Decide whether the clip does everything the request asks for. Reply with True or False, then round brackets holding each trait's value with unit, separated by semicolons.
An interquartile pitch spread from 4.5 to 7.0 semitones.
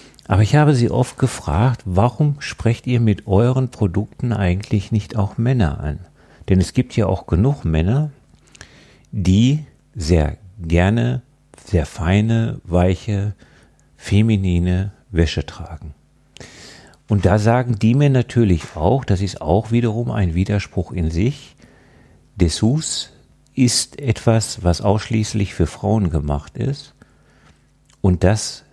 True (5.1 semitones)